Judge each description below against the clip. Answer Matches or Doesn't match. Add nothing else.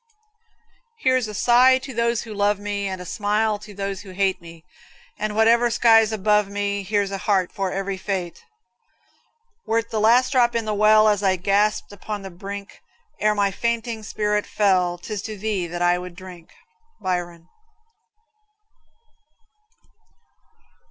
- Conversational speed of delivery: Matches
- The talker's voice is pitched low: Doesn't match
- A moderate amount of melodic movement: Doesn't match